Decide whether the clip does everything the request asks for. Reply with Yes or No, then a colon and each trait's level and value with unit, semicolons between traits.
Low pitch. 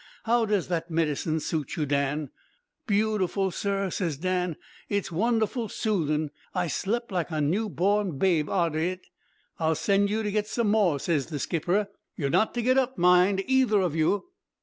No: medium, 185 Hz